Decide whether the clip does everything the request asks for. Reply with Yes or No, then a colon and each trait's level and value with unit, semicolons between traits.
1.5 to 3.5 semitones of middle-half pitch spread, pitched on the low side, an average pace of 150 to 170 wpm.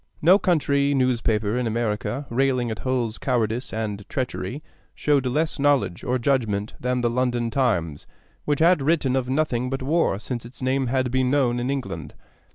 Yes: average, 2.8 semitones; low, 125 Hz; average, 165 wpm